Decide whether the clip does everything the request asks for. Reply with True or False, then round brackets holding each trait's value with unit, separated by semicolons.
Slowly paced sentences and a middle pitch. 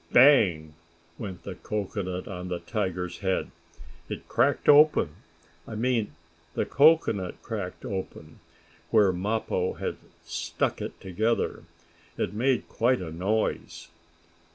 False (115 wpm; 100 Hz)